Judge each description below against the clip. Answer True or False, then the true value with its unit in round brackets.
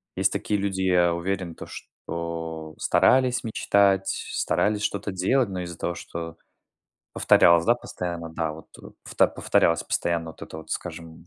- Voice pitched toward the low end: True (85 Hz)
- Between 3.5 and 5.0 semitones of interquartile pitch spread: False (2.9 semitones)